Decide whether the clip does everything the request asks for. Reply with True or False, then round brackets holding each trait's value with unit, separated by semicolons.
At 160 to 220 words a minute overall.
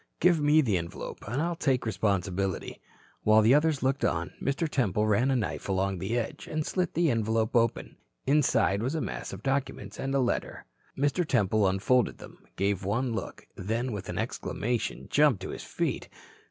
True (180 wpm)